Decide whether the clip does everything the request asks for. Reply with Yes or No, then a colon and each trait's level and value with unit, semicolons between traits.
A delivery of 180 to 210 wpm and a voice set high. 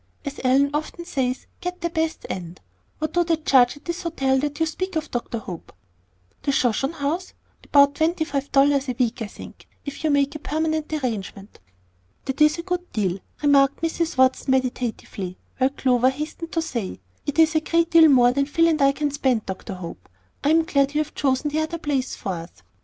Yes: average, 200 wpm; very high, 285 Hz